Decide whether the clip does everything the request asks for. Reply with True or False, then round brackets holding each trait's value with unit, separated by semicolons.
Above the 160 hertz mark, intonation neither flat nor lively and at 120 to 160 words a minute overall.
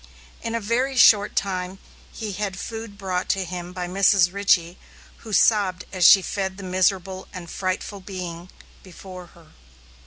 False (190 Hz; 1.8 semitones; 155 wpm)